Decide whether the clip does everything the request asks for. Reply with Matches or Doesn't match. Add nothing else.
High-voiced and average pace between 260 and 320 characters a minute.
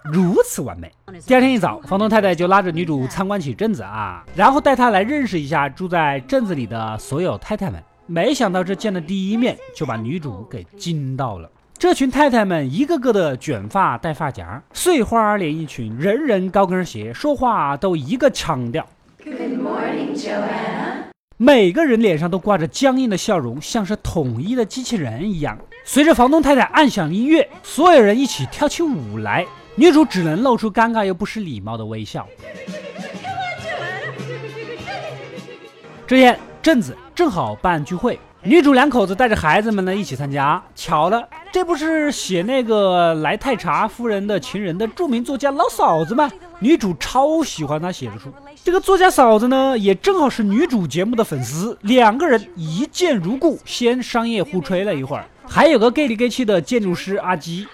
Matches